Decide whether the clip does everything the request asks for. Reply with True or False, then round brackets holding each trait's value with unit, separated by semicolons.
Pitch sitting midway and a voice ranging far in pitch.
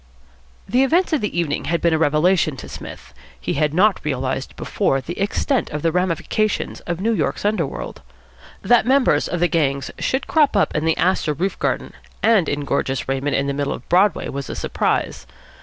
True (170 Hz; 6.3 semitones)